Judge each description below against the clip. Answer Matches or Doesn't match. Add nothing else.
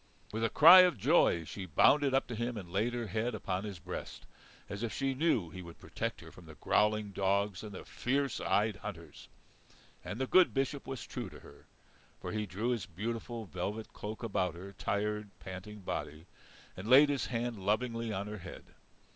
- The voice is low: Matches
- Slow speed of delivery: Doesn't match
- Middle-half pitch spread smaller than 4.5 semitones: Matches